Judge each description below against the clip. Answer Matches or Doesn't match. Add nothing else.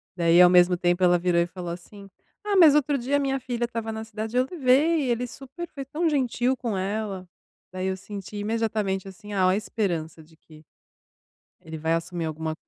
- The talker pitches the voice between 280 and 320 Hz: Doesn't match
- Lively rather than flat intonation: Matches